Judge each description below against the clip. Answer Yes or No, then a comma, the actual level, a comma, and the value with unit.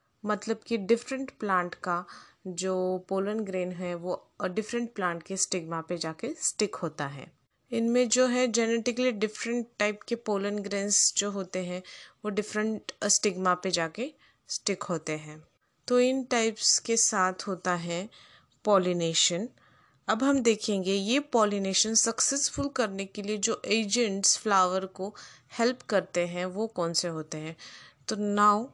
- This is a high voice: Yes, high, 205 Hz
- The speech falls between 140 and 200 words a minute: Yes, average, 145 wpm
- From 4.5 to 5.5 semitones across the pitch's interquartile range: No, average, 3.9 semitones